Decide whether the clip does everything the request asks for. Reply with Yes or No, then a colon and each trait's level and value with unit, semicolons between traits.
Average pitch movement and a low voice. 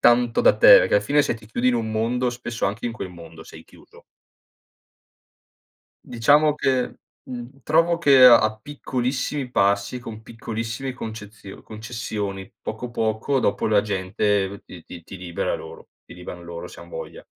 Yes: average, 3.8 semitones; low, 115 Hz